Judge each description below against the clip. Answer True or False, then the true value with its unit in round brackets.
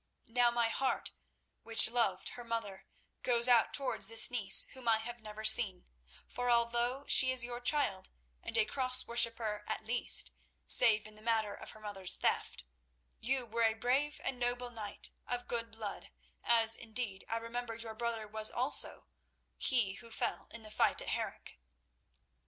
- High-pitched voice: True (230 Hz)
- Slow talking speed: False (165 wpm)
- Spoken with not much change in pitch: True (2.1 semitones)